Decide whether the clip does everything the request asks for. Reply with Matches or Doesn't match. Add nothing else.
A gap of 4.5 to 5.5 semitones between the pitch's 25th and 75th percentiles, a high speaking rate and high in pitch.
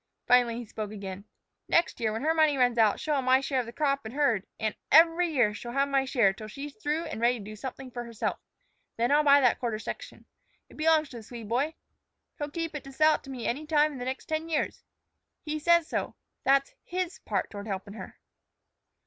Matches